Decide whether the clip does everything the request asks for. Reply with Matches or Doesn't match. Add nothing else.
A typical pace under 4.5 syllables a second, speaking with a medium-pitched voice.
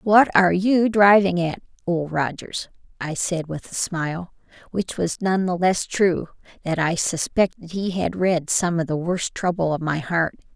Matches